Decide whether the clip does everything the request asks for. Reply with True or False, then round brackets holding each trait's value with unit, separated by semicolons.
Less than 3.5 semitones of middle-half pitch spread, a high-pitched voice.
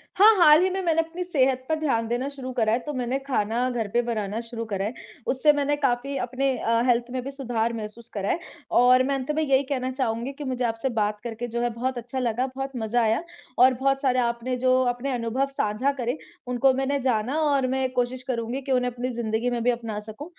True (2.6 semitones; 250 Hz)